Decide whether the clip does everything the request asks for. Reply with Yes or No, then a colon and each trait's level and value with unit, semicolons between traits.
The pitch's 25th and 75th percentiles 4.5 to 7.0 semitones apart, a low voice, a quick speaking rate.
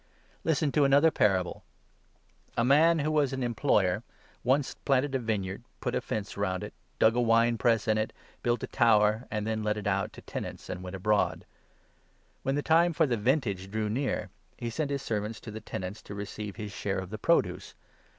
Yes: average, 4.8 semitones; low, 110 Hz; fast, 220 wpm